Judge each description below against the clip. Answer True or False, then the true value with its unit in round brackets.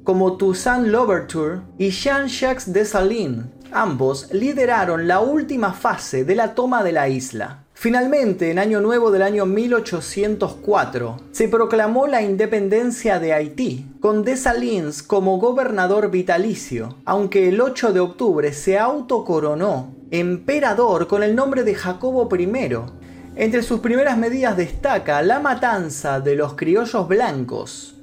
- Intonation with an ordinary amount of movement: False (6.1 semitones)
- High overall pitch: True (200 Hz)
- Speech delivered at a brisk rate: False (130 wpm)